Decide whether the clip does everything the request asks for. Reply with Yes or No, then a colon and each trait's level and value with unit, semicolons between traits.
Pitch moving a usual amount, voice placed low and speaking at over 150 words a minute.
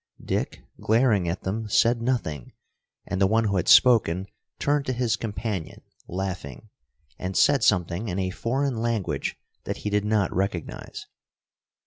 No: average, 3.9 semitones; low, 105 Hz; average, 145 wpm